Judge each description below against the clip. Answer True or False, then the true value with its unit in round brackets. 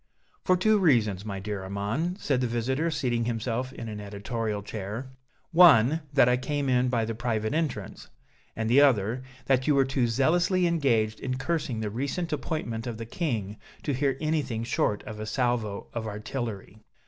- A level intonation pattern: False (4.5 semitones)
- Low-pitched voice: True (120 Hz)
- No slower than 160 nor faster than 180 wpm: True (175 wpm)